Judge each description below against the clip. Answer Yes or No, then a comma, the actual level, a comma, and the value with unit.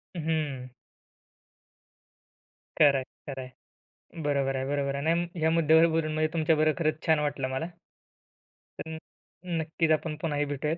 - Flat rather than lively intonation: Yes, narrow, 2.2 semitones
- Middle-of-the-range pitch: Yes, medium, 155 Hz